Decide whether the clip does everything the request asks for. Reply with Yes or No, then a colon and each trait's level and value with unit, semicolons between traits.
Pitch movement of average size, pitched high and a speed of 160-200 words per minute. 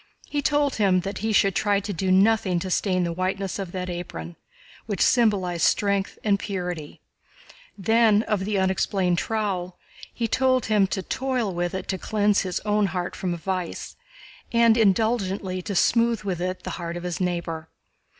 Yes: average, 3.0 semitones; high, 195 Hz; average, 170 wpm